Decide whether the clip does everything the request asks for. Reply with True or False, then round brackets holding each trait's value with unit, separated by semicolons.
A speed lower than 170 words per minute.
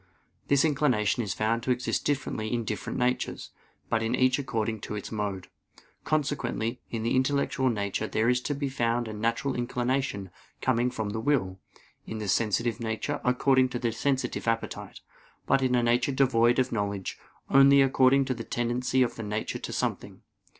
False (175 wpm)